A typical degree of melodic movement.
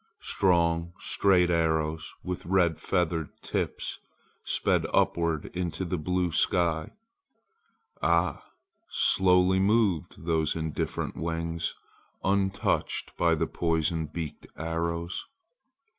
No: narrow, 1.9 semitones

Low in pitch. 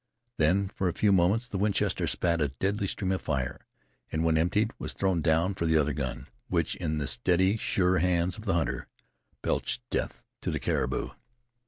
Yes: very low, 90 Hz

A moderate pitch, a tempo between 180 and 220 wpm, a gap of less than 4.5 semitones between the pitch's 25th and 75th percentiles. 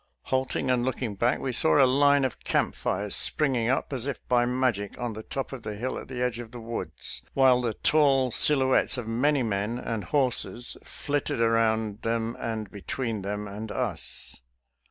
No: low, 120 Hz; average, 190 wpm; average, 3.0 semitones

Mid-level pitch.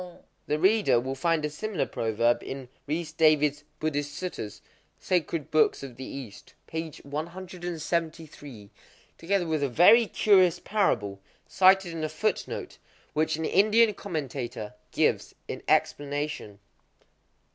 Yes: medium, 155 Hz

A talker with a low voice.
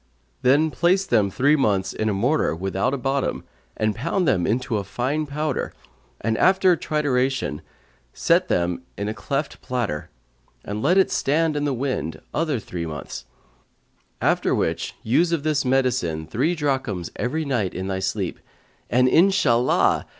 Yes: low, 130 Hz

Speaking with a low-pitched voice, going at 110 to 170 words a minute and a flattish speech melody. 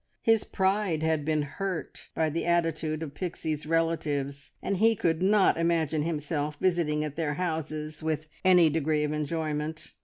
No: medium, 160 Hz; average, 155 wpm; narrow, 2.1 semitones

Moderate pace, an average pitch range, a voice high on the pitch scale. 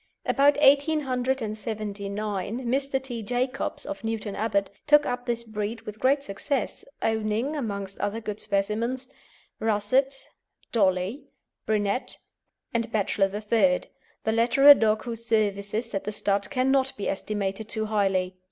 No: slow, 130 wpm; average, 3.9 semitones; high, 220 Hz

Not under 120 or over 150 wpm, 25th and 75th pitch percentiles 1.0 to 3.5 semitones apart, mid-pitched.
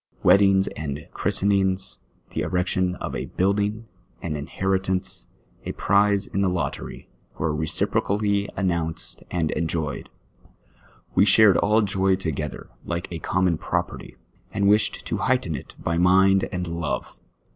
No: slow, 135 wpm; average, 2.9 semitones; very low, 95 Hz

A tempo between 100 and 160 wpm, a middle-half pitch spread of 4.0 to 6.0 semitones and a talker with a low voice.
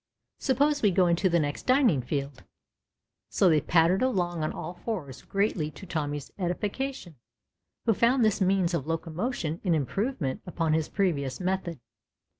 No: average, 150 wpm; average, 4.8 semitones; medium, 175 Hz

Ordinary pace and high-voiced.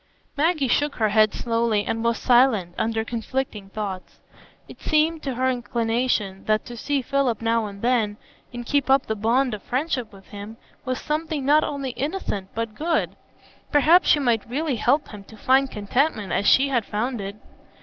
Yes: average, 180 wpm; high, 240 Hz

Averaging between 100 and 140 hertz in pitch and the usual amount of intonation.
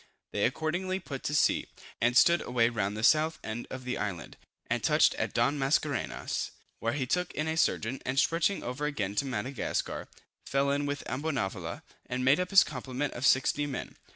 Yes: low, 135 Hz; average, 3.7 semitones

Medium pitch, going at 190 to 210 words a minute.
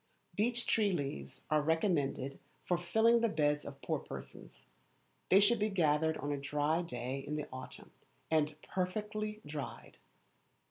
No: medium, 160 Hz; average, 145 wpm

